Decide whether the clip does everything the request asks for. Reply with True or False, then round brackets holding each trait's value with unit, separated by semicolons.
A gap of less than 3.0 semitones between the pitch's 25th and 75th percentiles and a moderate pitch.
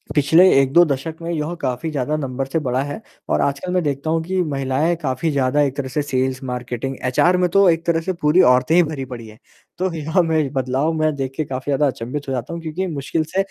False (3.8 semitones; 145 Hz)